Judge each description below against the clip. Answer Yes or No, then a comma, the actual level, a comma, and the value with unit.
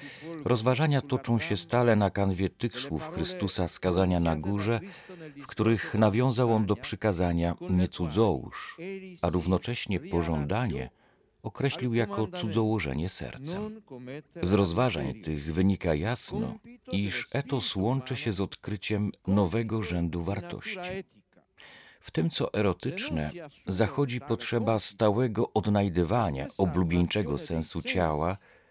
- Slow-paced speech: Yes, slow, 105 wpm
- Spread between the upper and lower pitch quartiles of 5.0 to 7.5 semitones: Yes, wide, 5.5 semitones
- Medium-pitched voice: No, low, 110 Hz